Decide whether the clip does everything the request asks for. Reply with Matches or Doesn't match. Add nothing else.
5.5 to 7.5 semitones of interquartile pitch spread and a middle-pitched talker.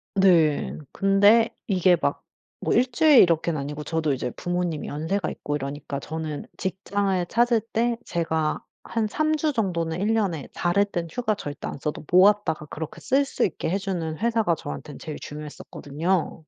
Doesn't match